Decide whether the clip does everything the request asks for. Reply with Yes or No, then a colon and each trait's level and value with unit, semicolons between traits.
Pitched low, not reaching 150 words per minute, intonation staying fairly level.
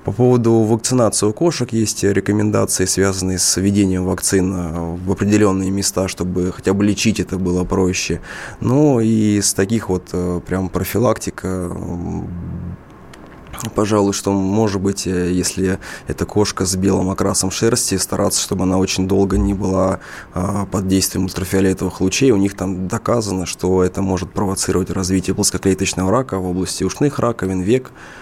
Yes: very low, 95 Hz; average, 140 wpm; narrow, 1.8 semitones